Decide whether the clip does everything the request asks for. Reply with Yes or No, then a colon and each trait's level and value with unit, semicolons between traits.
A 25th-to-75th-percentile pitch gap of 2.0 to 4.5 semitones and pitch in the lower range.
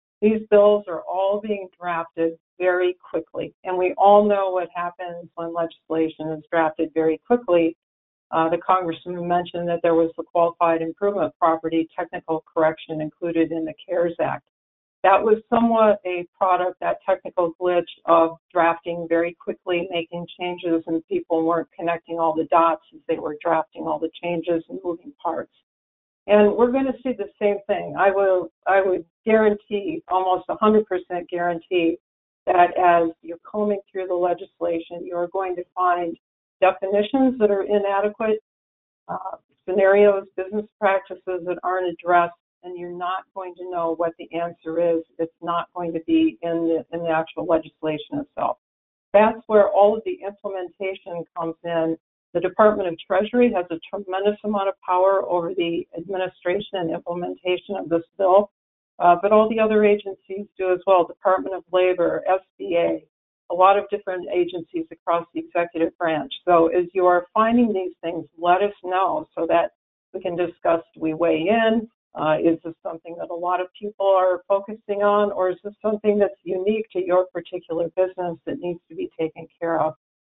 No: average, 2.9 semitones; medium, 180 Hz